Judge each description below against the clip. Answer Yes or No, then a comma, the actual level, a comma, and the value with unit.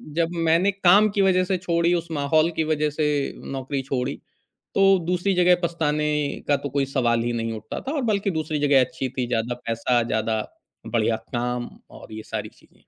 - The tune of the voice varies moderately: No, wide, 6.3 semitones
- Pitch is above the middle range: No, medium, 150 Hz